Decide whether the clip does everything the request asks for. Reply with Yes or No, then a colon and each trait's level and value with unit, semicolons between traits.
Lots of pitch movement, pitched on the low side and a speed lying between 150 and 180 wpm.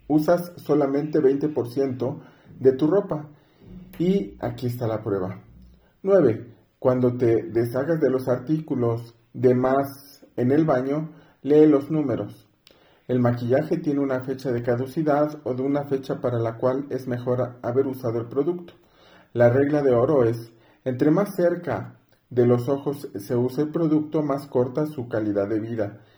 No: average, 3.8 semitones; low, 130 Hz; average, 155 wpm